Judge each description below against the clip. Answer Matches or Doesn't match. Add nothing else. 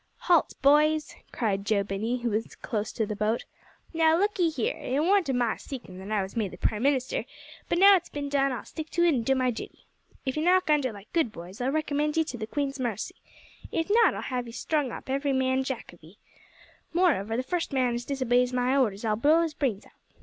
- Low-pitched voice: Doesn't match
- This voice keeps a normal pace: Doesn't match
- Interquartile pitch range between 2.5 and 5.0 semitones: Doesn't match